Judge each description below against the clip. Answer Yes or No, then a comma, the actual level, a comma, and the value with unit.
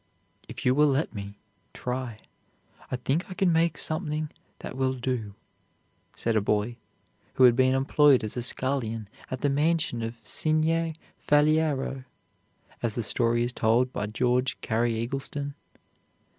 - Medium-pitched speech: No, low, 130 Hz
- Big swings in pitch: No, average, 4.0 semitones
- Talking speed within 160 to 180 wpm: No, average, 145 wpm